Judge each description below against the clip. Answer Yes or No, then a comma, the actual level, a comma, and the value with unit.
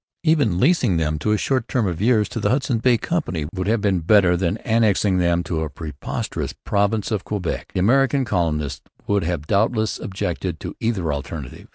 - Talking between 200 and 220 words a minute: No, average, 190 wpm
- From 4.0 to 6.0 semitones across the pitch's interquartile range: Yes, average, 4.9 semitones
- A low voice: Yes, low, 100 Hz